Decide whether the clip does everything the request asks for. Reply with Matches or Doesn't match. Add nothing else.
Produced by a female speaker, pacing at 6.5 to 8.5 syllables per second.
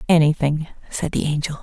Doesn't match